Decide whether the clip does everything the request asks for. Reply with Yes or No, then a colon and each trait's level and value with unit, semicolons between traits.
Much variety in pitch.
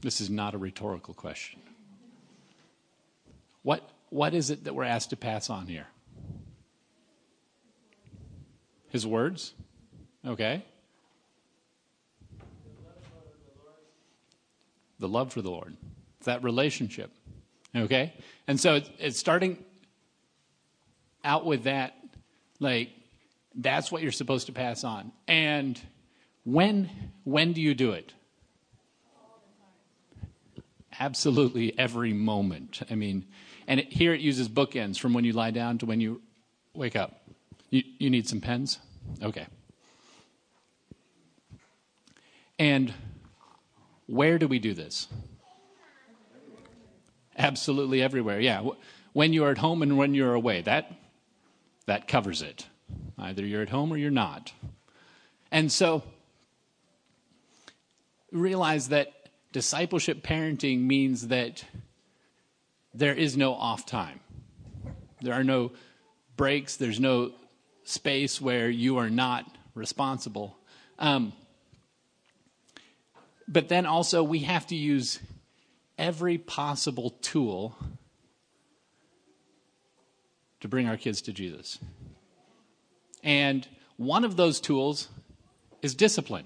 No: average, 4.6 semitones